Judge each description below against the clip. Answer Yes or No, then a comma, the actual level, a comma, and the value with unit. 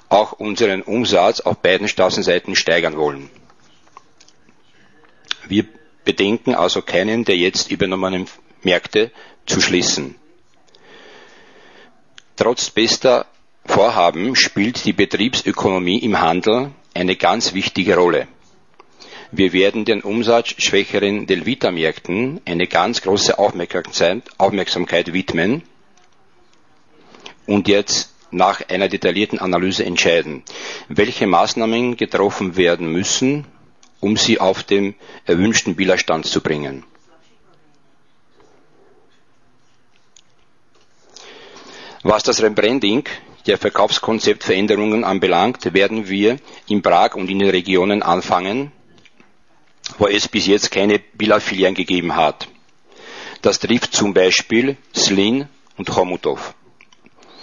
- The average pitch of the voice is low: Yes, low, 100 Hz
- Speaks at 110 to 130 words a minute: No, slow, 95 wpm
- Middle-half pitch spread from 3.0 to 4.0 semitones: Yes, average, 3.5 semitones